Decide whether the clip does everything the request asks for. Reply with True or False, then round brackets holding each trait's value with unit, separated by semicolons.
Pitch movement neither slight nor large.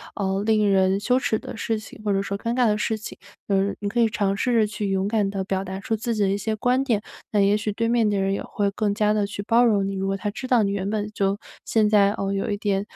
False (1.9 semitones)